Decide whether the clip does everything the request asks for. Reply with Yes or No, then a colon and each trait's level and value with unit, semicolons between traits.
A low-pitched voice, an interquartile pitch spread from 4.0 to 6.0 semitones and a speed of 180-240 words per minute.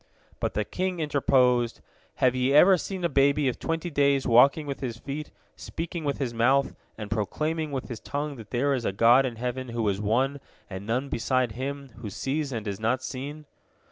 No: low, 130 Hz; average, 3.4 semitones; average, 200 wpm